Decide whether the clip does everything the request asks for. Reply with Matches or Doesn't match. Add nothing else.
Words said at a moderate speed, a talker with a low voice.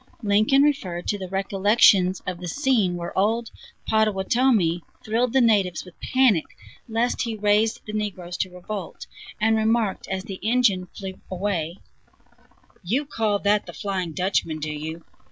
Doesn't match